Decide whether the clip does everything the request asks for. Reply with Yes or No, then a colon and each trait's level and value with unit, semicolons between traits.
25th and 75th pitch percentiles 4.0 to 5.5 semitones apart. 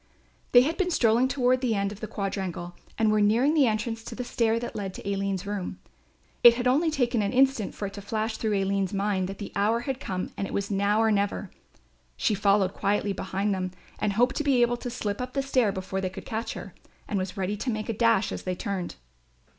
No: average, 3.5 semitones